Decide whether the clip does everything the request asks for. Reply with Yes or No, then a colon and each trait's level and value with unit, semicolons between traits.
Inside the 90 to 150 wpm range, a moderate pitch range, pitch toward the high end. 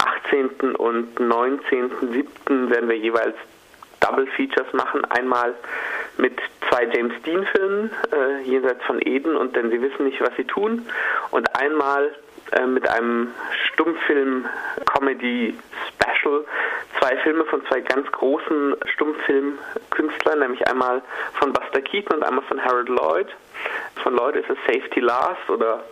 No: average, 130 wpm; average, 4.1 semitones; low, 135 Hz